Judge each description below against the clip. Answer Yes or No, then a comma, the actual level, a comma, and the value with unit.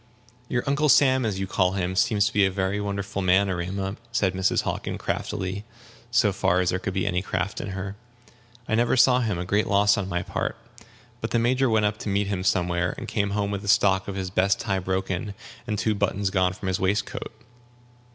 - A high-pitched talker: No, low, 100 Hz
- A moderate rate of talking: No, fast, 220 wpm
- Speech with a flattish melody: Yes, narrow, 1.9 semitones